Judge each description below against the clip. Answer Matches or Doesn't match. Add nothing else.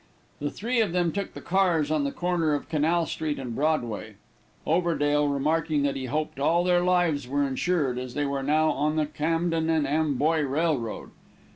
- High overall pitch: Doesn't match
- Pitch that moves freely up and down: Doesn't match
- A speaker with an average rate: Matches